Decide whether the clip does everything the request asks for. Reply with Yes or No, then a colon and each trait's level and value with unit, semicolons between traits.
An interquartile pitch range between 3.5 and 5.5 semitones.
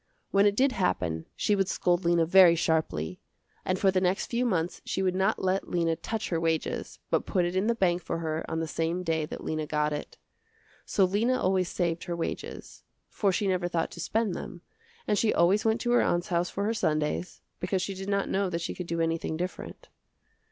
No: average, 3.0 semitones